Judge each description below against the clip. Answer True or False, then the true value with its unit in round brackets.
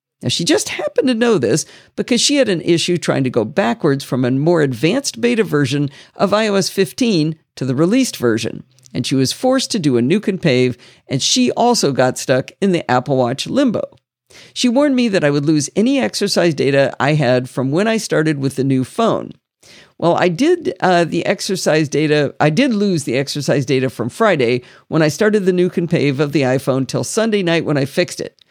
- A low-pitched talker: False (155 Hz)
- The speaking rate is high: True (215 wpm)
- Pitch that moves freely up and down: True (7.4 semitones)